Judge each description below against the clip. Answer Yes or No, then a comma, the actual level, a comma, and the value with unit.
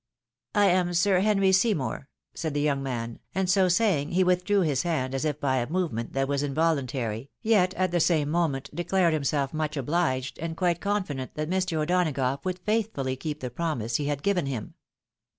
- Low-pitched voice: No, medium, 155 Hz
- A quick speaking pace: No, average, 190 wpm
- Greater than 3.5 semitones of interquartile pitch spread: Yes, average, 4.9 semitones